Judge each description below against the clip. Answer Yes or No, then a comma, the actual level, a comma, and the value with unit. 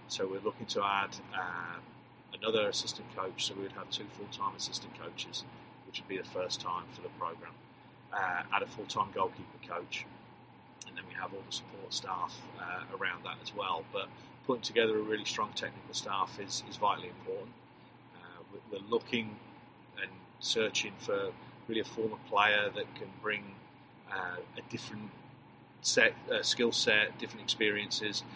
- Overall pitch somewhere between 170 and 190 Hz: No, low, 115 Hz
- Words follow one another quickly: No, average, 165 wpm